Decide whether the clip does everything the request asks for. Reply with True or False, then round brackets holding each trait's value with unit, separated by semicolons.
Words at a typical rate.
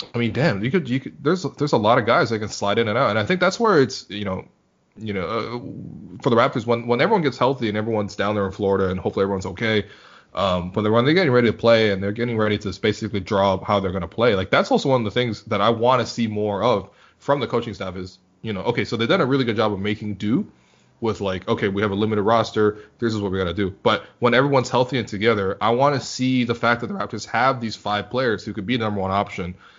False (280 wpm)